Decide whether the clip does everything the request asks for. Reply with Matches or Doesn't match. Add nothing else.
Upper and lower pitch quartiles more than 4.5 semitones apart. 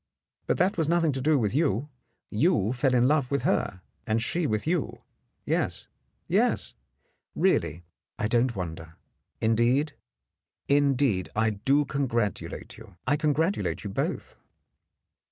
Matches